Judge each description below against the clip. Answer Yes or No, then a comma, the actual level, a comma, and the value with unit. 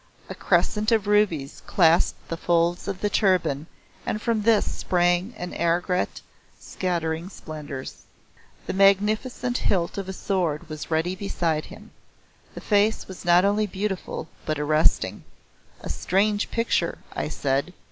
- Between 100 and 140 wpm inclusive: Yes, slow, 135 wpm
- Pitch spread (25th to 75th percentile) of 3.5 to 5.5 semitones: Yes, average, 4.2 semitones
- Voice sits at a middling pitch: Yes, medium, 180 Hz